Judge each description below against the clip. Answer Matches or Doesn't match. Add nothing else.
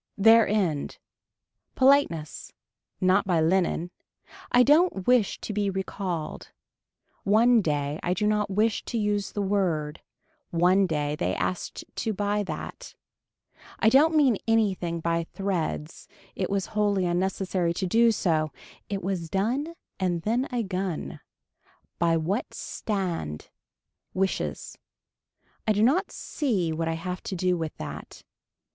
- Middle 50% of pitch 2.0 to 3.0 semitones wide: Doesn't match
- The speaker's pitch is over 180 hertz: Matches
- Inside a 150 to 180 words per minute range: Doesn't match